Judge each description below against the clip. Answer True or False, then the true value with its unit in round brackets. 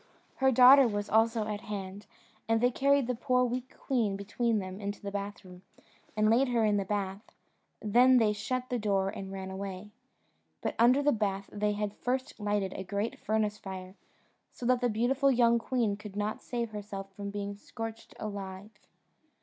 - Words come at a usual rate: True (180 wpm)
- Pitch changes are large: False (3.2 semitones)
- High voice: True (210 Hz)